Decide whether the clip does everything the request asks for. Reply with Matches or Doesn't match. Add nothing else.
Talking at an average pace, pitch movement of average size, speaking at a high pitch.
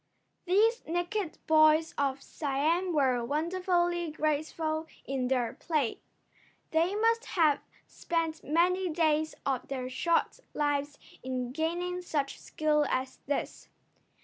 Doesn't match